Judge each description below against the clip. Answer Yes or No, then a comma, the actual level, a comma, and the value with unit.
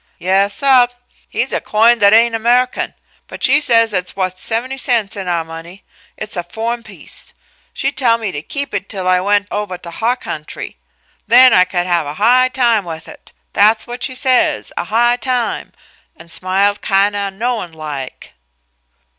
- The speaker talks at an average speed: Yes, average, 180 wpm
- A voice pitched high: Yes, high, 210 Hz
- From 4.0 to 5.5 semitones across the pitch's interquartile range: Yes, average, 4.7 semitones